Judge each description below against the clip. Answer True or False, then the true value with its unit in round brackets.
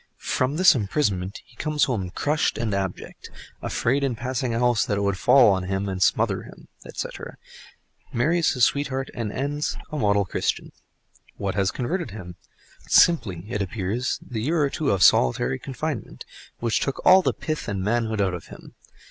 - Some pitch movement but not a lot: False (6.0 semitones)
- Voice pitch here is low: True (115 Hz)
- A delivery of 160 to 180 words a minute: True (165 wpm)